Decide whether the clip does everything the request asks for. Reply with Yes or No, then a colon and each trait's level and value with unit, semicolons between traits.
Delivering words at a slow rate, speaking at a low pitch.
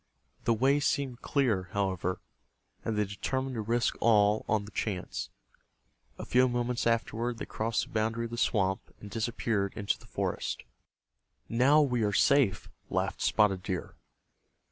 No: average, 150 wpm; low, 115 Hz